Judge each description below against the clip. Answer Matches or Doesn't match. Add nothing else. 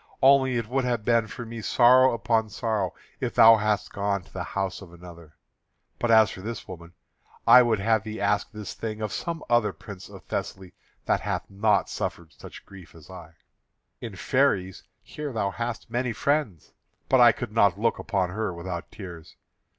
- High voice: Doesn't match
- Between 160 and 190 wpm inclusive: Matches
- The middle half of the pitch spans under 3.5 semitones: Doesn't match